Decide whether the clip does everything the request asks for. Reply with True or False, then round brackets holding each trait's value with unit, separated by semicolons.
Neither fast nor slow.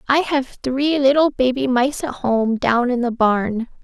True (190 wpm)